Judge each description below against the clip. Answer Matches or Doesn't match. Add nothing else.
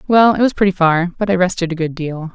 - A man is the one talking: Doesn't match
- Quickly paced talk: Matches